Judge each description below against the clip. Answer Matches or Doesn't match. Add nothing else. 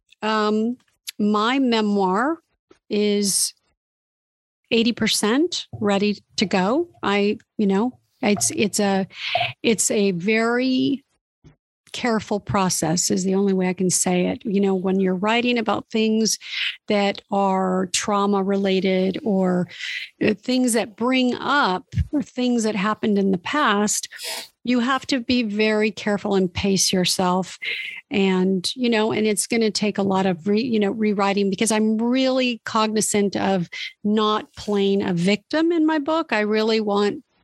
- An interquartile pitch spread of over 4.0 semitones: Doesn't match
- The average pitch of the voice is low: Doesn't match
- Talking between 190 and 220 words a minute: Doesn't match